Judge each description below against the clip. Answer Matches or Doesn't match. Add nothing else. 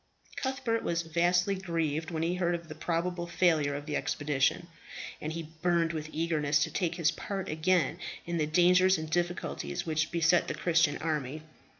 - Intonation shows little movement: Matches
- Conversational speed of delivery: Matches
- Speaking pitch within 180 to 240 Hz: Doesn't match